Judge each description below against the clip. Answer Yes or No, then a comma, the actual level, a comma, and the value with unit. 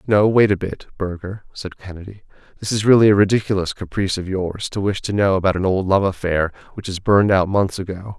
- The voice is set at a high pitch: No, very low, 95 Hz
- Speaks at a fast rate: Yes, fast, 220 wpm